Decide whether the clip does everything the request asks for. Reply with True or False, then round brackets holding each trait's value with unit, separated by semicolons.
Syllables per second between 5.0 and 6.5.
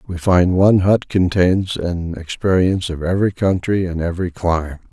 True (5.2 syllables/s)